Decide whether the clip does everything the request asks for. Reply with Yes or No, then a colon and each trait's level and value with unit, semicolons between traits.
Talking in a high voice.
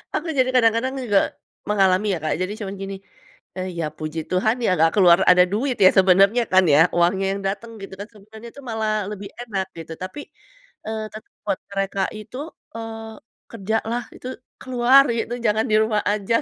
Yes: high, 210 Hz